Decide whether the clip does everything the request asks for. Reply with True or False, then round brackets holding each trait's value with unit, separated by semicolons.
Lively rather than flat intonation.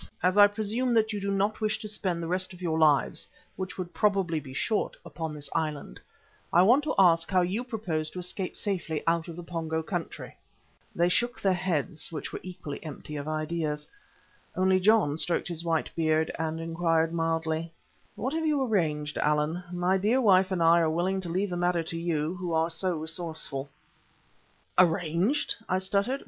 False (3.1 semitones)